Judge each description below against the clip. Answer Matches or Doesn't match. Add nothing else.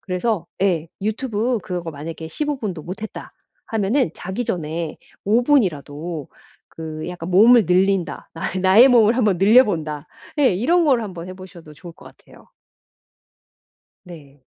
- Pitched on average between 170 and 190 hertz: Matches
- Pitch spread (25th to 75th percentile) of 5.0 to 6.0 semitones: Matches